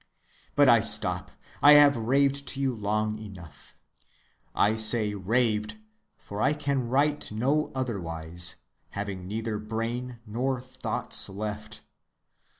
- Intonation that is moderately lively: Yes, average, 4.0 semitones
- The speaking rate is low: Yes, slow, 120 wpm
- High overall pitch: No, low, 110 Hz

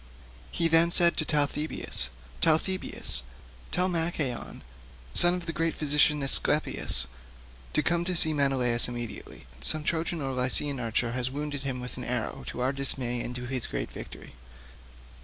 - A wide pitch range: No, average, 4.6 semitones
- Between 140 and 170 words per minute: Yes, average, 160 wpm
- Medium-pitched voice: Yes, medium, 145 Hz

